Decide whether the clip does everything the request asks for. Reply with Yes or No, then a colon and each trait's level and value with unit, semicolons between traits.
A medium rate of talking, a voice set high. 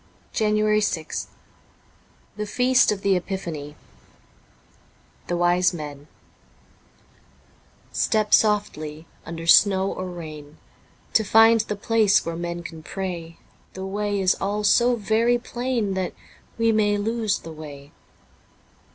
No: slow, 120 wpm; high, 195 Hz